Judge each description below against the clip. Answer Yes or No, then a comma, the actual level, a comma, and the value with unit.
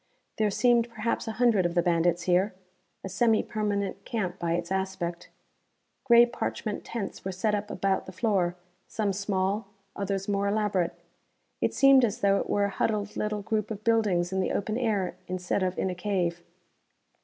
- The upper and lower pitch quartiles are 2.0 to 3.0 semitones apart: Yes, average, 2.7 semitones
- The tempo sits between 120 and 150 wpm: No, average, 180 wpm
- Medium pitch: No, high, 200 Hz